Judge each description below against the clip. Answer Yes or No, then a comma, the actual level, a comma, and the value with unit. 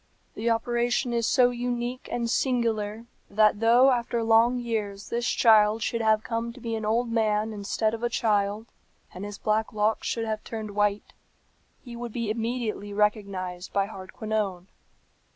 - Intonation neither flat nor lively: No, narrow, 2.1 semitones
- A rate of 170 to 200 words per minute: No, average, 160 wpm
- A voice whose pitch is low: No, high, 220 Hz